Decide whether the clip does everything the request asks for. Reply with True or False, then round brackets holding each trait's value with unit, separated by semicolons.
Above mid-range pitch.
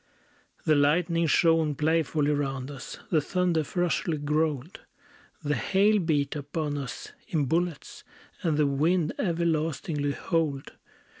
False (155 Hz)